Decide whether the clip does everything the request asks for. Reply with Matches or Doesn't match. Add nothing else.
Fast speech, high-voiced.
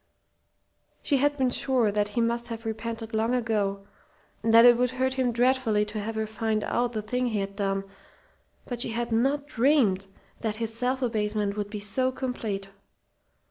Doesn't match